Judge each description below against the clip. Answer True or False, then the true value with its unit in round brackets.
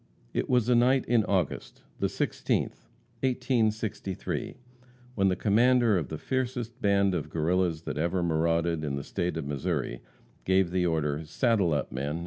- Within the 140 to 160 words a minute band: True (155 wpm)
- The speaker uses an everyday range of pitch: False (6.1 semitones)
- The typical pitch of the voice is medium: False (90 Hz)